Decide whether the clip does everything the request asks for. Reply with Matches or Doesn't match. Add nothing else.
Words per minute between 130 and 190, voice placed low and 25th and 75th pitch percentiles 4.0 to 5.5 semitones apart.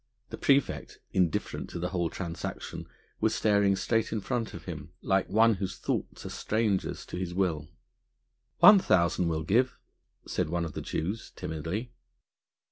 Matches